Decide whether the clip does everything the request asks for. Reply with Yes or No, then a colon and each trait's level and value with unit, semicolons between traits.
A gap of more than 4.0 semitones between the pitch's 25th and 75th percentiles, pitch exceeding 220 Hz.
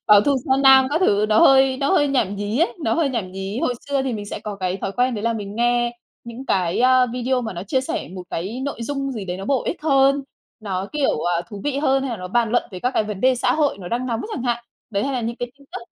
Yes: average, 4.6 semitones; high, 240 Hz